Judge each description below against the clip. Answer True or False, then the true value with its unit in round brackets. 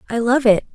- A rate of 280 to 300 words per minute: False (240 wpm)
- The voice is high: True (235 Hz)